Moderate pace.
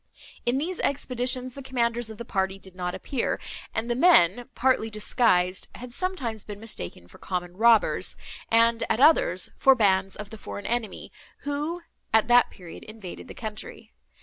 Yes: average, 165 wpm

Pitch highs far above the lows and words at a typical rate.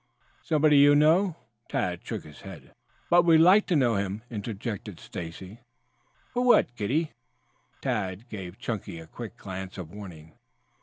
Yes: wide, 8.1 semitones; average, 150 wpm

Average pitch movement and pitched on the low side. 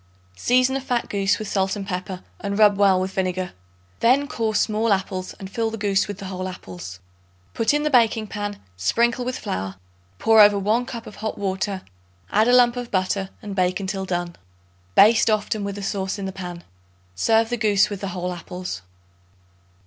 No: average, 3.0 semitones; high, 200 Hz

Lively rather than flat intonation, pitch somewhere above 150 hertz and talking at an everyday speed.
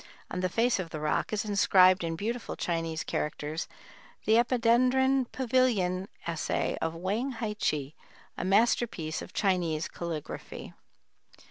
No: wide, 6.0 semitones; high, 190 Hz; slow, 130 wpm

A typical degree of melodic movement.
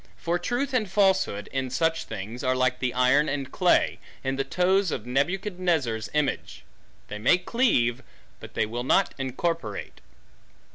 No: wide, 6.5 semitones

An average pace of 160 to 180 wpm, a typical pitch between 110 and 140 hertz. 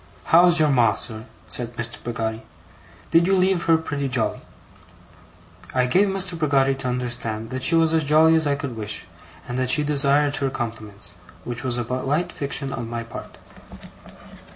Yes: average, 175 wpm; low, 135 Hz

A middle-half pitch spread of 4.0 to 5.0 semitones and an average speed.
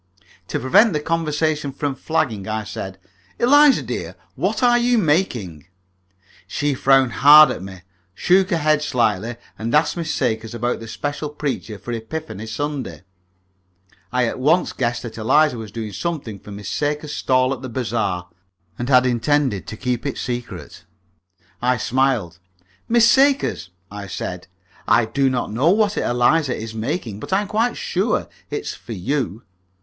No: wide, 5.5 semitones; average, 160 wpm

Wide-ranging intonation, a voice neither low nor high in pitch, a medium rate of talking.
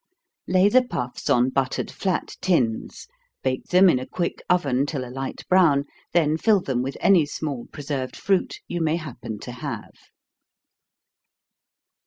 Yes: wide, 5.8 semitones; medium, 145 Hz; average, 150 wpm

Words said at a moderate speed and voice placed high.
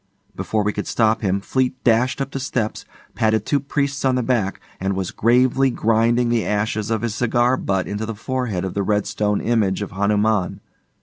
No: average, 195 wpm; low, 110 Hz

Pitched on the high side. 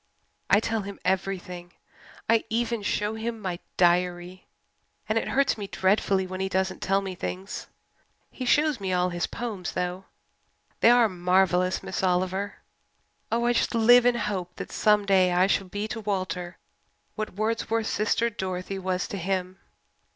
Yes: high, 195 Hz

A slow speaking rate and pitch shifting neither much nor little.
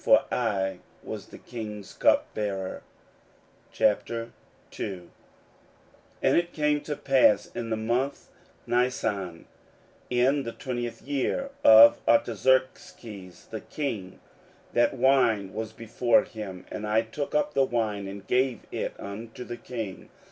Yes: slow, 120 wpm; average, 3.9 semitones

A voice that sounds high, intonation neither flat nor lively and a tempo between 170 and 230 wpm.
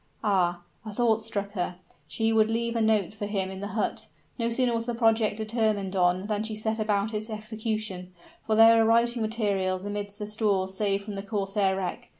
No: high, 215 Hz; narrow, 2.1 semitones; average, 200 wpm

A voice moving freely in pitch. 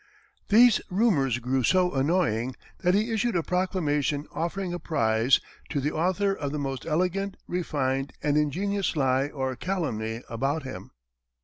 Yes: wide, 5.7 semitones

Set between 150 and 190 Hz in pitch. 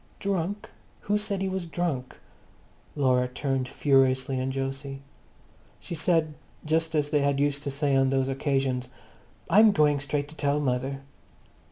No: medium, 140 Hz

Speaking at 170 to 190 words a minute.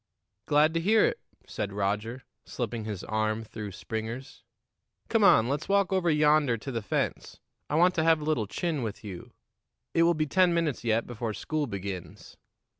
Yes: average, 180 wpm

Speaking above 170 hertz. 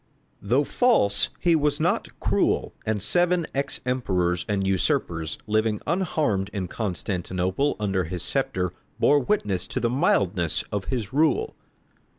No: low, 105 Hz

